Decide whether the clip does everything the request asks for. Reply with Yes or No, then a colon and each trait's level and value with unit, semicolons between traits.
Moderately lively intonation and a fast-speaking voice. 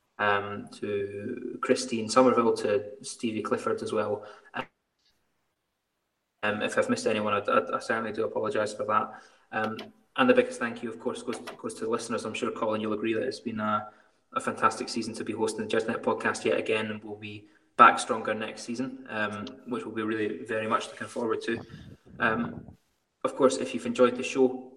No: average, 3.4 semitones; average, 195 wpm